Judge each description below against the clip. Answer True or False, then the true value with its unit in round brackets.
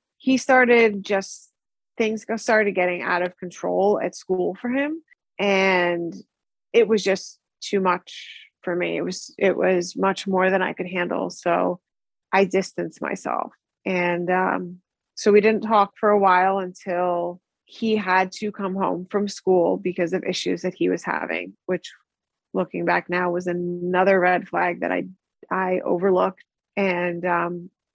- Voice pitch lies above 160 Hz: True (185 Hz)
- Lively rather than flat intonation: False (2.5 semitones)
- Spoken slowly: False (155 wpm)